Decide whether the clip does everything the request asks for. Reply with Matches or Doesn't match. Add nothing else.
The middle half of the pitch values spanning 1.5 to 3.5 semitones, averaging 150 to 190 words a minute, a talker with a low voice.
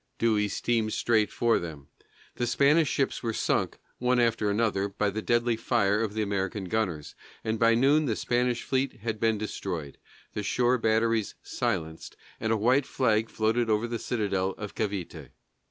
Matches